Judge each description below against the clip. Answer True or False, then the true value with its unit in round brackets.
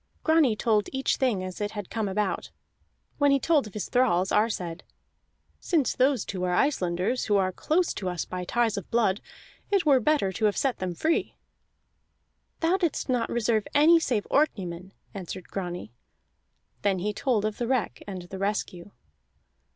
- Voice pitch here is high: True (210 Hz)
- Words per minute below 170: False (175 wpm)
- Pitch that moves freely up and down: True (6.0 semitones)